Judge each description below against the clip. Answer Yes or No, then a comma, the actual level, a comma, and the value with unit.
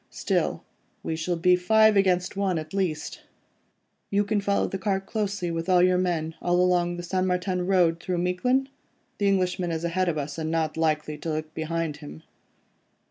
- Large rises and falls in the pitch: No, average, 2.7 semitones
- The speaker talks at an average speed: Yes, average, 180 wpm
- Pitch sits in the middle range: Yes, medium, 180 Hz